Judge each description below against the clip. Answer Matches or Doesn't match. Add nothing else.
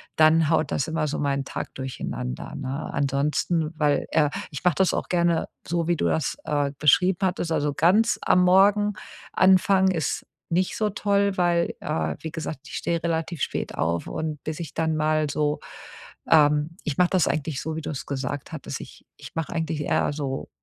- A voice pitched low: Doesn't match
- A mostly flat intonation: Doesn't match